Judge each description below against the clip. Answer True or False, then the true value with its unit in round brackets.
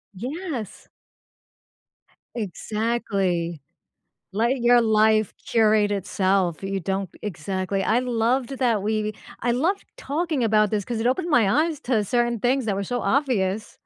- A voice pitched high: True (220 Hz)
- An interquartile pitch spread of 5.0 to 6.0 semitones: False (3.7 semitones)